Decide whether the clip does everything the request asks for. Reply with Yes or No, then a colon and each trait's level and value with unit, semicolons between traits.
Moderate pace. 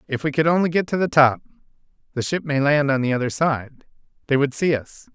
No: fast, 210 wpm